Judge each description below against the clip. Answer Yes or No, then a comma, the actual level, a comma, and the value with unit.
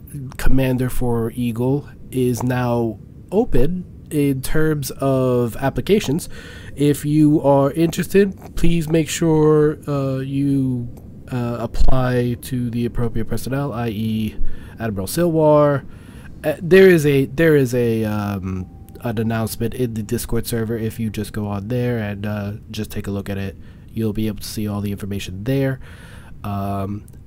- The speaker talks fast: No, average, 145 wpm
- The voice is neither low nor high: No, low, 120 Hz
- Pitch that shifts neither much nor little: Yes, average, 4.5 semitones